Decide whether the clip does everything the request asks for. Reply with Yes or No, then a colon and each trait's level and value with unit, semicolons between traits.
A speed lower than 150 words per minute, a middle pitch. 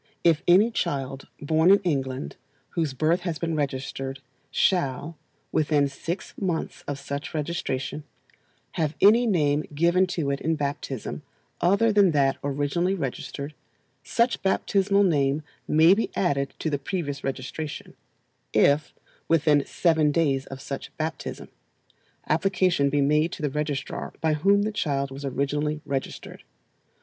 Yes: slow, 135 wpm; medium, 150 Hz